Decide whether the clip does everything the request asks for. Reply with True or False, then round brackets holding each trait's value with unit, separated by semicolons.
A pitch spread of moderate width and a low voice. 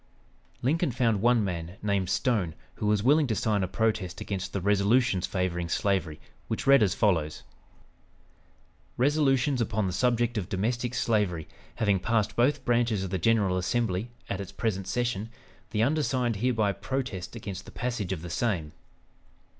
True (4.3 semitones; 105 Hz)